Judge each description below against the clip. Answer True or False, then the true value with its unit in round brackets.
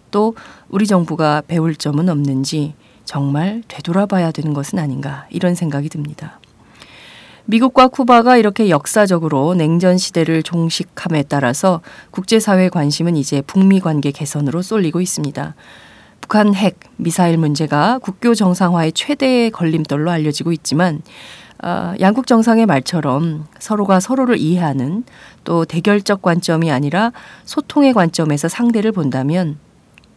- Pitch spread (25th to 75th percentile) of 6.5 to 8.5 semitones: False (5.3 semitones)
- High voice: False (170 Hz)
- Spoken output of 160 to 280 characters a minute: False (310 characters per minute)